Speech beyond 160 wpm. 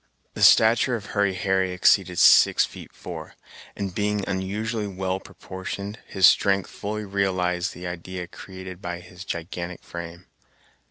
No: average, 140 wpm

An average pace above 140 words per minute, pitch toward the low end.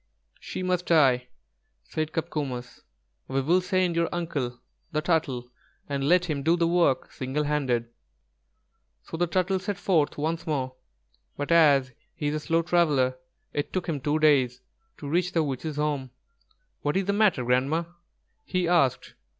No: average, 160 wpm; medium, 155 Hz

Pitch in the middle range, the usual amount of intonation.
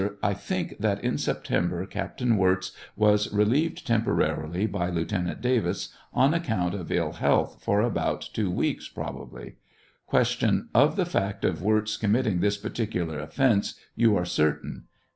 No: low, 105 Hz; average, 4.5 semitones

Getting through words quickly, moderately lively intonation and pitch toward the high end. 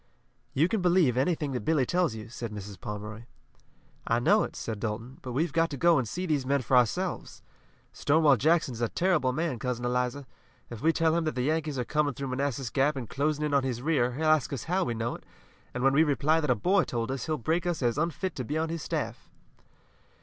No: fast, 235 wpm; average, 4.7 semitones; medium, 140 Hz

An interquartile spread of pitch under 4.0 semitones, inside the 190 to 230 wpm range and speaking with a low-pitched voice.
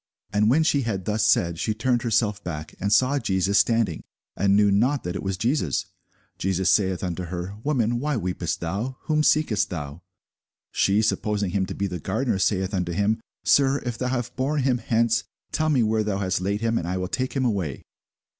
No: average, 4.4 semitones; average, 200 wpm; low, 105 Hz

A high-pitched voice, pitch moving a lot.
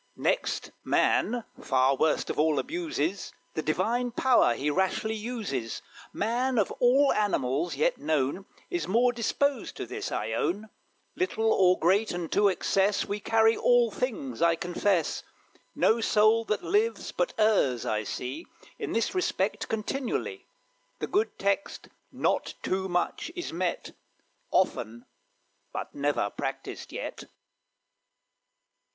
Yes: high, 205 Hz; wide, 7.1 semitones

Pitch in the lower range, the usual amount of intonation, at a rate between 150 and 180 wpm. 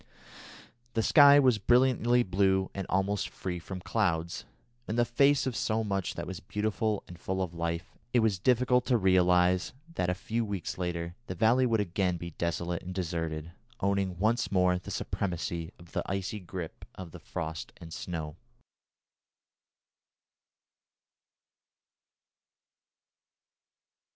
No: very low, 95 Hz; average, 4.1 semitones; slow, 135 wpm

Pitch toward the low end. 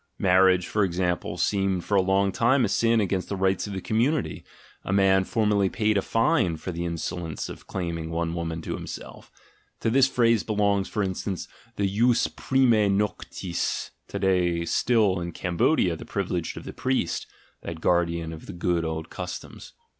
Yes: very low, 95 Hz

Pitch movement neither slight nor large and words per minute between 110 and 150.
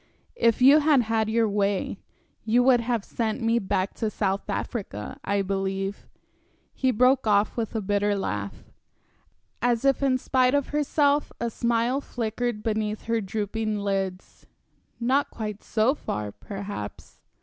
Yes: average, 3.5 semitones; average, 145 wpm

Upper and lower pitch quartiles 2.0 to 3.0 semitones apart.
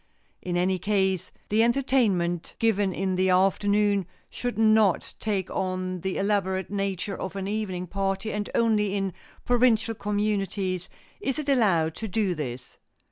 Yes: narrow, 2.6 semitones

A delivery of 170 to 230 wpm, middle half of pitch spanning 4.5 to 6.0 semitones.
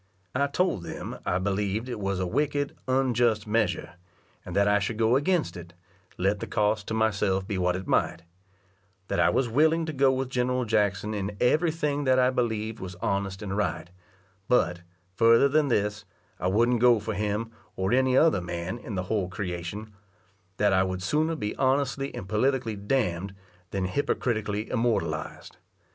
Yes: average, 175 wpm; average, 4.8 semitones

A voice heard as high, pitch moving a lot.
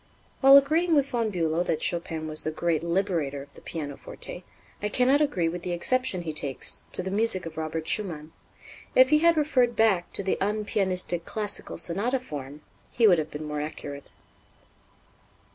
No: medium, 180 Hz; wide, 6.9 semitones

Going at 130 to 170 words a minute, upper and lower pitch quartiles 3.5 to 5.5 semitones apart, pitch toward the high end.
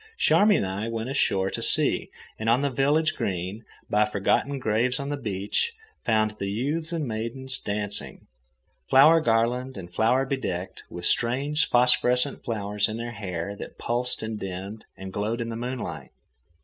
No: average, 160 wpm; average, 4.3 semitones; low, 115 Hz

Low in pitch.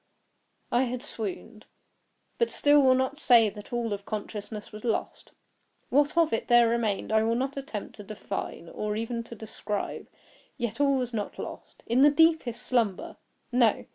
No: high, 235 Hz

